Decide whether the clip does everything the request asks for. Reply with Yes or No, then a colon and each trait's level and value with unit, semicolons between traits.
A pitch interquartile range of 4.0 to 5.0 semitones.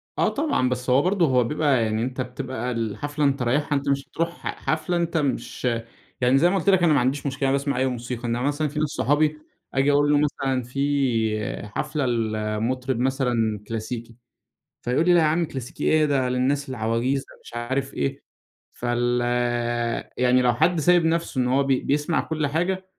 No: average, 3.4 semitones